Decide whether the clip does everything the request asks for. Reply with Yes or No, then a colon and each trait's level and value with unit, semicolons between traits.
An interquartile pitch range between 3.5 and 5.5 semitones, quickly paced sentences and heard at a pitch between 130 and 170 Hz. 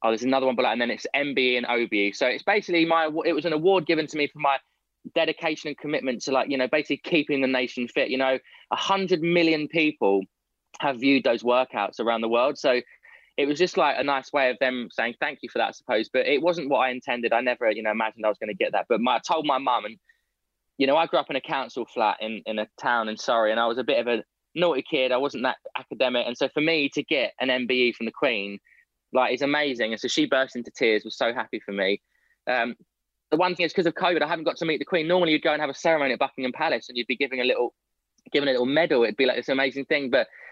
Yes: average, 4.6 semitones; fast, 275 wpm; low, 135 Hz